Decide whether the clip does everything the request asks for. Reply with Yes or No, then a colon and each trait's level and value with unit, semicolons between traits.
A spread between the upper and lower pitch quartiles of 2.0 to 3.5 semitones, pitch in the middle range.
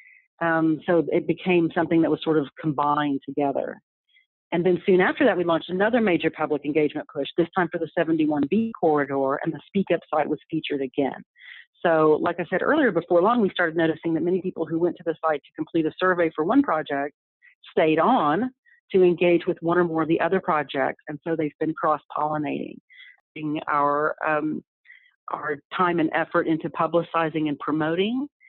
Yes: average, 2.8 semitones; medium, 165 Hz